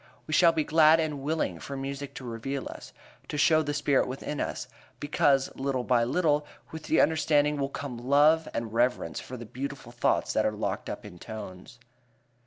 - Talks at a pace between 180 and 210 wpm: Yes, average, 190 wpm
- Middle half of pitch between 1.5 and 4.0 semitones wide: Yes, average, 3.4 semitones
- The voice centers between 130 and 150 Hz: Yes, medium, 140 Hz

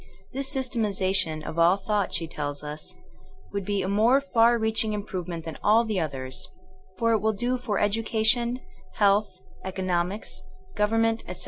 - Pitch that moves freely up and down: No, average, 3.9 semitones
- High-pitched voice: Yes, high, 205 Hz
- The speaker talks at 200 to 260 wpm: No, average, 180 wpm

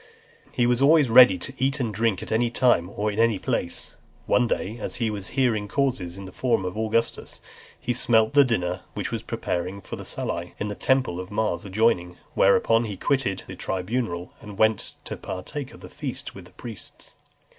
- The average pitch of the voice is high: No, low, 110 Hz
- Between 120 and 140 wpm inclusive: No, fast, 205 wpm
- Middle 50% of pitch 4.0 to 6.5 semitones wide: Yes, average, 4.4 semitones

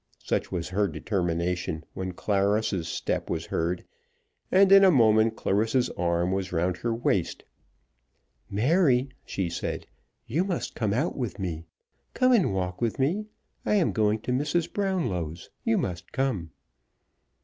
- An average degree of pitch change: No, wide, 7.2 semitones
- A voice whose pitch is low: Yes, low, 105 Hz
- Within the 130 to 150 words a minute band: Yes, average, 145 wpm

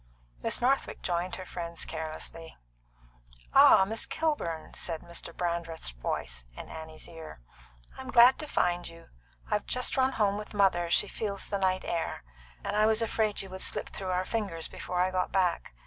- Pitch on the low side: No, medium, 185 Hz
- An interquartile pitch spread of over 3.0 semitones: Yes, average, 4.1 semitones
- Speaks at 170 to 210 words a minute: Yes, average, 175 wpm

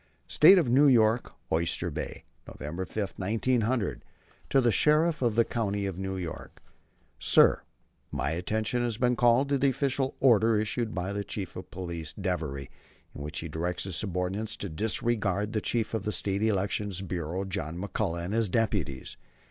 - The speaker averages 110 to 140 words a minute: No, average, 165 wpm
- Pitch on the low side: Yes, low, 105 Hz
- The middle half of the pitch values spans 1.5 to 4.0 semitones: No, average, 4.6 semitones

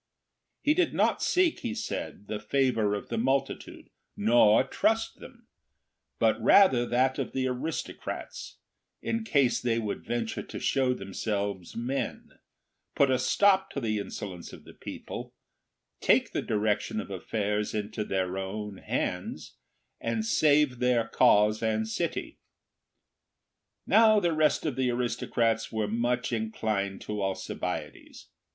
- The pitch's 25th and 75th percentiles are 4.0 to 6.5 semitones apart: Yes, average, 4.3 semitones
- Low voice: Yes, low, 115 Hz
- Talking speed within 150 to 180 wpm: No, slow, 135 wpm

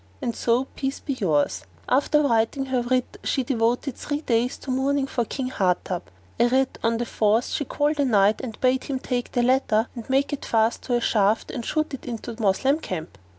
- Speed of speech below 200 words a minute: No, fast, 205 wpm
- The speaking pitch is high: Yes, high, 245 Hz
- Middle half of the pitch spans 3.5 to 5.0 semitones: No, average, 3.0 semitones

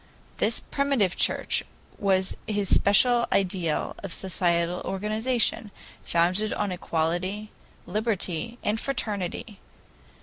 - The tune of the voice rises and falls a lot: No, average, 3.4 semitones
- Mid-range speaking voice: No, high, 200 Hz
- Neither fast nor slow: No, slow, 95 wpm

